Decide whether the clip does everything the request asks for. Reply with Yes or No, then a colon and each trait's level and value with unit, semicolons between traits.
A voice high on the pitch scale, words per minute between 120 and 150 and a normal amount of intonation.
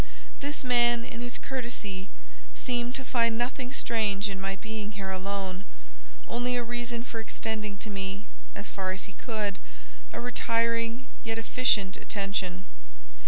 Yes: high, 225 Hz; average, 145 wpm; average, 3.4 semitones